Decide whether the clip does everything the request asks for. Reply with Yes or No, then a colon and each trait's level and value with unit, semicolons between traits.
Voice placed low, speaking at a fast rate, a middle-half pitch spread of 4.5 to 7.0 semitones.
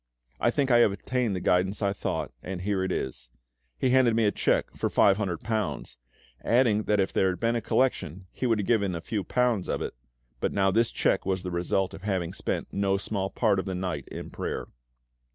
No: low, 100 Hz; fast, 215 wpm; average, 3.4 semitones